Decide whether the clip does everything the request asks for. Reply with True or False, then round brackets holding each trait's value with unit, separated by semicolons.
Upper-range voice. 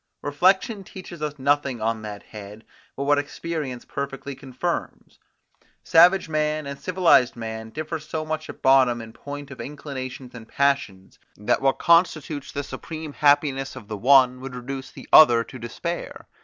False (140 Hz)